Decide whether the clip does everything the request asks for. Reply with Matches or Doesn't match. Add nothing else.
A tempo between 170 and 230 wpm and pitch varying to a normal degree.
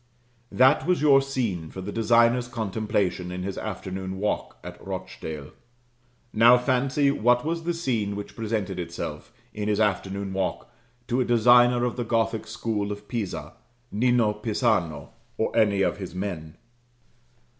Doesn't match